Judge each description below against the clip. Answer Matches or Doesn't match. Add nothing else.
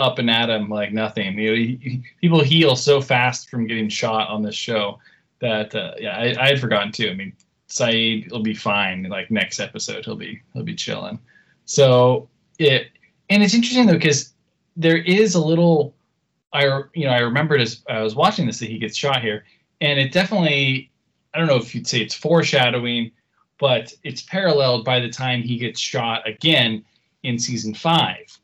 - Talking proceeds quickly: Doesn't match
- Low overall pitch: Matches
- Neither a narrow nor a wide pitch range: Doesn't match